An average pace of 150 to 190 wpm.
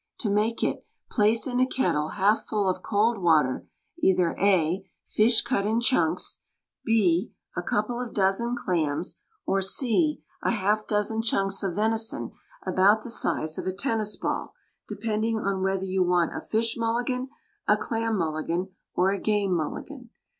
Yes: average, 165 wpm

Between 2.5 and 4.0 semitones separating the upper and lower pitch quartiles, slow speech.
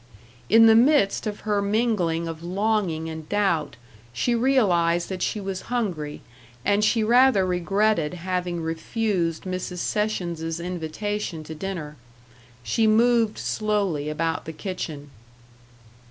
No: average, 4.6 semitones; slow, 125 wpm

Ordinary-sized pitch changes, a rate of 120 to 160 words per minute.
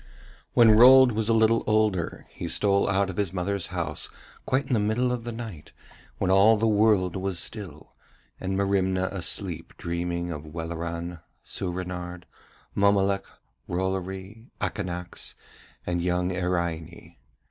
Yes: average, 3.4 semitones; slow, 135 wpm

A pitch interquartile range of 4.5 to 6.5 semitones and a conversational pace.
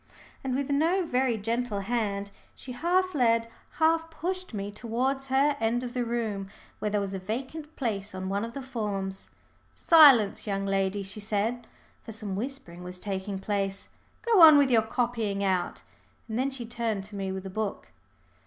Yes: average, 5.1 semitones; average, 180 wpm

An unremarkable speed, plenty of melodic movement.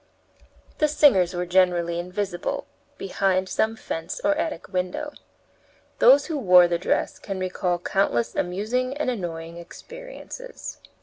No: slow, 125 wpm; wide, 7.2 semitones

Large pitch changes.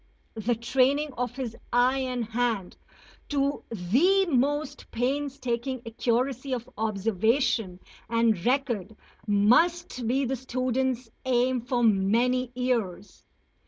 No: average, 2.7 semitones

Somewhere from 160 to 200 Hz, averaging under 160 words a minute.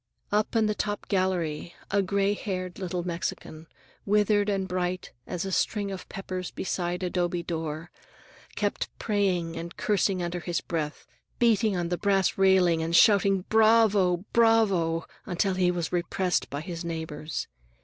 Yes: medium, 185 Hz; average, 150 wpm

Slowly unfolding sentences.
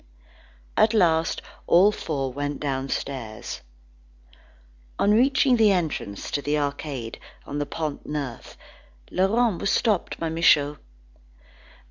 Yes: slow, 110 wpm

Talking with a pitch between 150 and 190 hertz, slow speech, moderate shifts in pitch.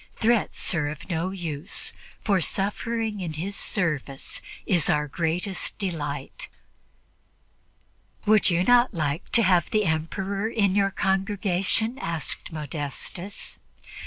Yes: medium, 185 Hz; slow, 115 wpm; average, 4.3 semitones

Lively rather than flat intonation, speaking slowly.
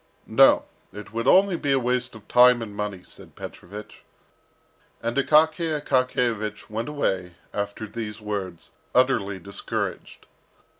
No: average, 4.1 semitones; slow, 130 wpm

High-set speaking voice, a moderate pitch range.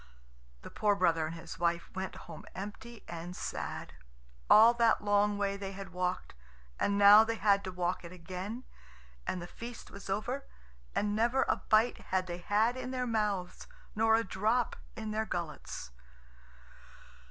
Yes: high, 205 Hz; average, 3.4 semitones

